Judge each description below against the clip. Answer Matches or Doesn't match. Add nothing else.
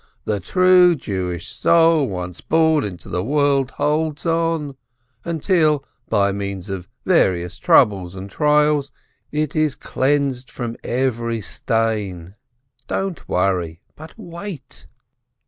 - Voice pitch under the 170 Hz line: Matches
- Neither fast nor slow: Doesn't match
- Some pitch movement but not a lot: Doesn't match